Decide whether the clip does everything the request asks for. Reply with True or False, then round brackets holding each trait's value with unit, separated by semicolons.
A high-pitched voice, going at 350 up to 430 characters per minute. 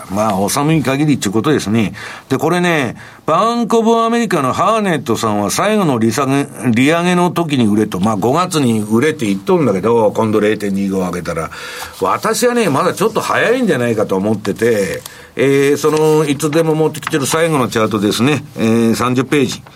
False (135 Hz; 380 characters per minute)